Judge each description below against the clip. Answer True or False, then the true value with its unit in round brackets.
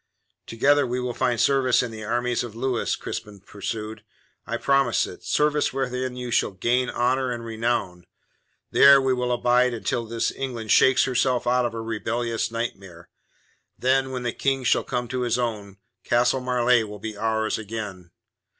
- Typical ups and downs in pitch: False (2.2 semitones)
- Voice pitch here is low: True (120 Hz)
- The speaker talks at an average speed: True (170 wpm)